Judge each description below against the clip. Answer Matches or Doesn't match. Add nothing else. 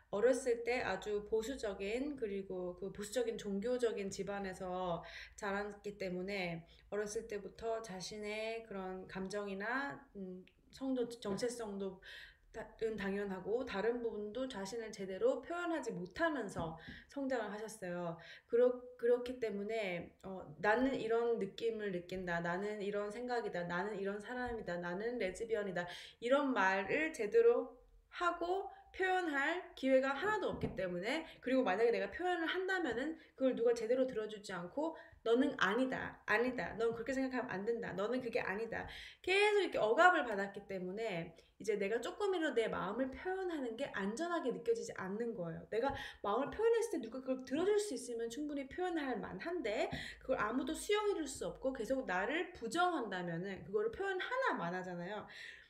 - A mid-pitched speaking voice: Doesn't match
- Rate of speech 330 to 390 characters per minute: Matches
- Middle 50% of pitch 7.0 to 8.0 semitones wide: Doesn't match